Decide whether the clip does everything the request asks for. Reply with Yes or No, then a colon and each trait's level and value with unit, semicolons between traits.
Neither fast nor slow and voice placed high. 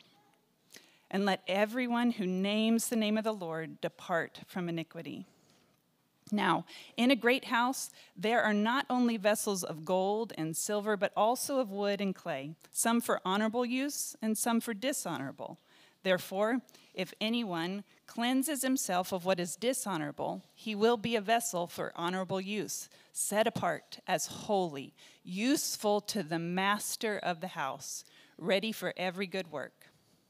Yes: average, 145 wpm; high, 210 Hz